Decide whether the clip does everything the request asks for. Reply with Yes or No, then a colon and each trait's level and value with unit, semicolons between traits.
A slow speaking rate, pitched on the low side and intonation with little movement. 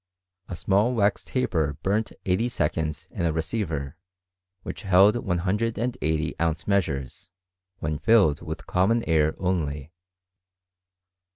No: slow, 110 wpm; very low, 90 Hz; average, 5.2 semitones